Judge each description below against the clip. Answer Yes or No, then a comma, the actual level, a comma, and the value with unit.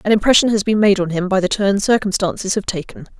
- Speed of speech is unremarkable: No, fast, 245 wpm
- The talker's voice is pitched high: Yes, high, 200 Hz